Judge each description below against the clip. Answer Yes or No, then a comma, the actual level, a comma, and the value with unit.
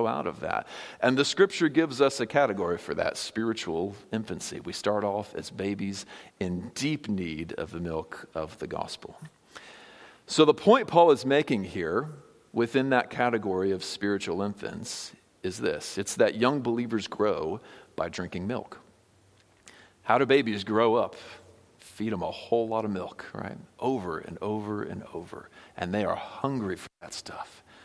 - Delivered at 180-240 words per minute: No, average, 165 wpm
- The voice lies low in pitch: Yes, low, 110 Hz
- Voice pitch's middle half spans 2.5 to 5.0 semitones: No, wide, 5.4 semitones